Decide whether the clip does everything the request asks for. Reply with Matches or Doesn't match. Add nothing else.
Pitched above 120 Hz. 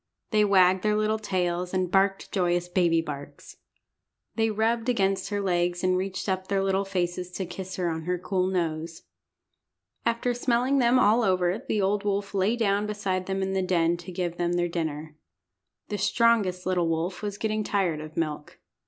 Matches